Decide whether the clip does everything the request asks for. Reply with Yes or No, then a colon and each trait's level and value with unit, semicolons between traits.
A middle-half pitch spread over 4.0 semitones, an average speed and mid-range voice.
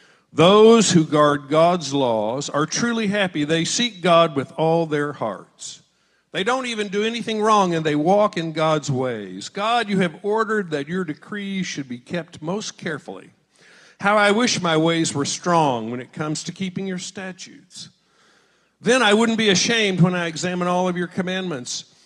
Yes: average, 4.9 semitones; average, 175 wpm; medium, 180 Hz